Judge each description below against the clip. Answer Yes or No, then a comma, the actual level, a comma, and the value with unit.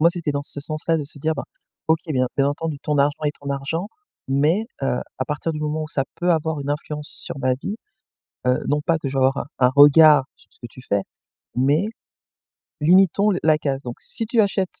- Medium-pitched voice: Yes, medium, 150 Hz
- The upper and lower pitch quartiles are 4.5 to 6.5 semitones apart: No, average, 2.8 semitones